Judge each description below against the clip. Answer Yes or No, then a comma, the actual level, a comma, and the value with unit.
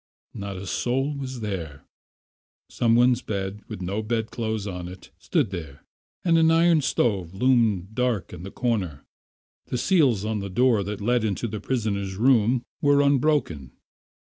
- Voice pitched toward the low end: Yes, low, 110 Hz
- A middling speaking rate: Yes, average, 155 wpm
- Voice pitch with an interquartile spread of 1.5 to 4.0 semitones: No, average, 4.7 semitones